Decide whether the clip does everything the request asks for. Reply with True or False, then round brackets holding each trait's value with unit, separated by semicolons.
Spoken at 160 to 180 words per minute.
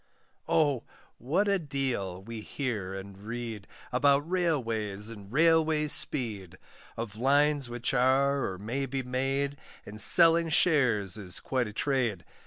False (135 wpm)